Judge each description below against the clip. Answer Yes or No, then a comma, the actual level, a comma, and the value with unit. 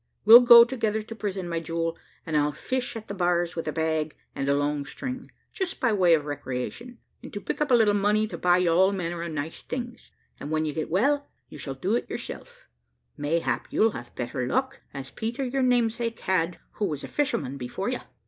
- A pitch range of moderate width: No, wide, 6.9 semitones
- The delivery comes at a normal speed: No, fast, 215 wpm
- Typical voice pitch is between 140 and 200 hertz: Yes, medium, 185 Hz